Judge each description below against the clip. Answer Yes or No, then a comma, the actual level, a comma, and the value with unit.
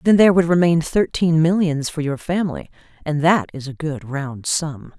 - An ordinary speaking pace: Yes, average, 190 wpm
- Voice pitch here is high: No, medium, 160 Hz